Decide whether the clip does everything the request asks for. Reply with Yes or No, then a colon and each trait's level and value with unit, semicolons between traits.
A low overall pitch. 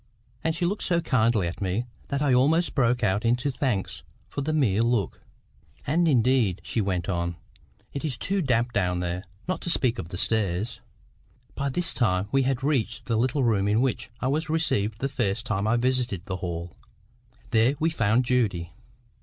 Yes: low, 120 Hz